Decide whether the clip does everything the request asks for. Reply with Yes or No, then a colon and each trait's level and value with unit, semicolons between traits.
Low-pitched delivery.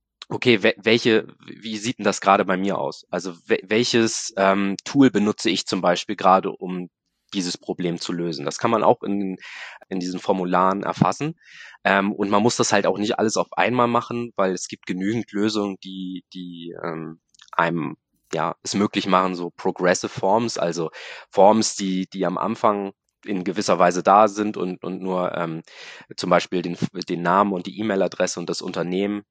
Yes: very low, 95 Hz